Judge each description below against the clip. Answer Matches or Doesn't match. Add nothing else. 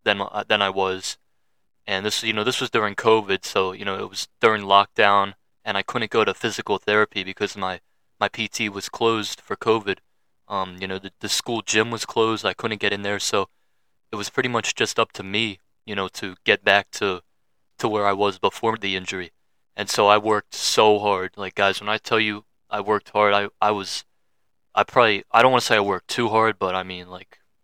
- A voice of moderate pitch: Doesn't match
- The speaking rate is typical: Doesn't match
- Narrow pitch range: Matches